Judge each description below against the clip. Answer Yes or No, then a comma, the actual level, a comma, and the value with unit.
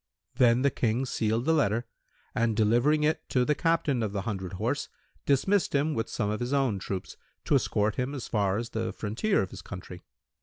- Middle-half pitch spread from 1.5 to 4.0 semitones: No, average, 4.8 semitones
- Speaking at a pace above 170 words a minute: Yes, average, 200 wpm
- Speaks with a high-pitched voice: No, low, 115 Hz